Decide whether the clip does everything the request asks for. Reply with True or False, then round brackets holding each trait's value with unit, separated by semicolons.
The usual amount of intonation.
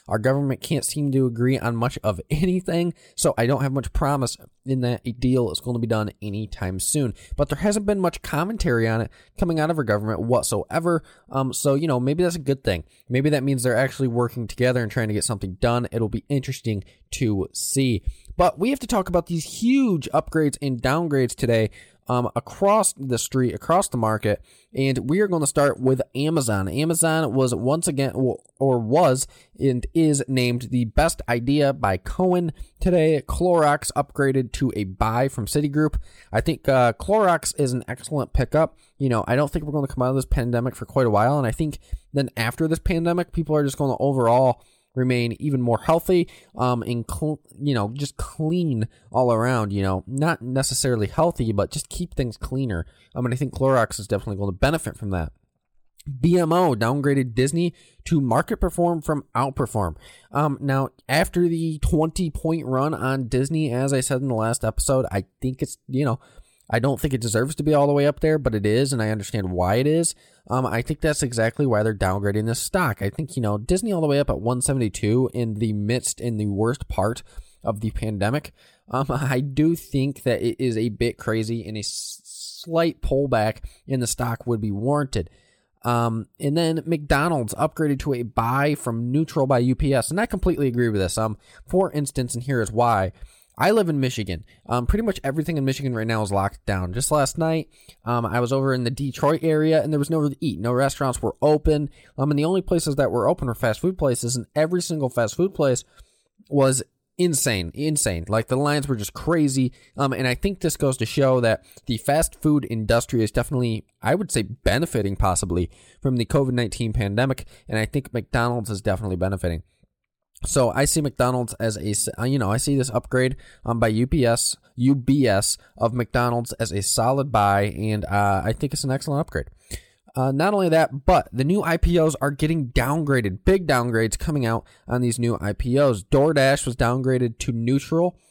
True (4.4 semitones)